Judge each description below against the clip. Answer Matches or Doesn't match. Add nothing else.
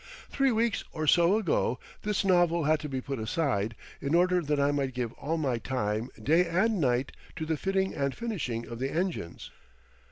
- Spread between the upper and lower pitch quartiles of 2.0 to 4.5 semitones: Doesn't match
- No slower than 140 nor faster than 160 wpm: Doesn't match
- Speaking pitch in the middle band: Matches